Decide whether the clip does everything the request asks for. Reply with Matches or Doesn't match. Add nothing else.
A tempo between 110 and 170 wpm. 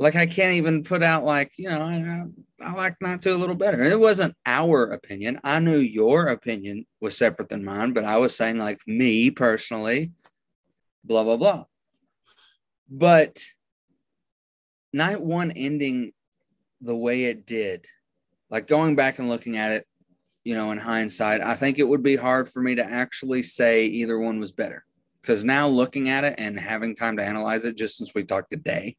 Doesn't match